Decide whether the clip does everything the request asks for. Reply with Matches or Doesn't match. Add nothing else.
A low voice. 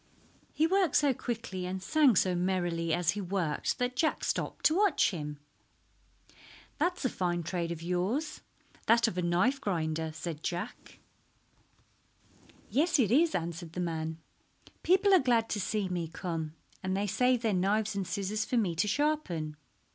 Doesn't match